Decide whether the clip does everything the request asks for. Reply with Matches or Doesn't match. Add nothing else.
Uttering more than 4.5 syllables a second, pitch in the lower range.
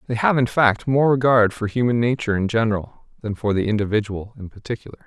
Matches